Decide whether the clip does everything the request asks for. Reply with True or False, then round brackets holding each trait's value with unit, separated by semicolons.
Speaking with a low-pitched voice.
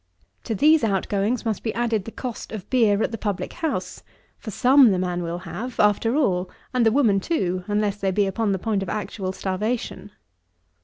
False (210 Hz)